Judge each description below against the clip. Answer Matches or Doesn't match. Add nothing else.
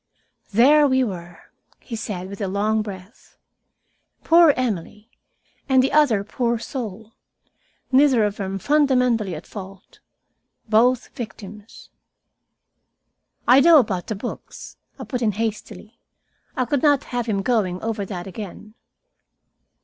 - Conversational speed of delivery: Doesn't match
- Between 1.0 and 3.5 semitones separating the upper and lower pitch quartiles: Doesn't match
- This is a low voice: Doesn't match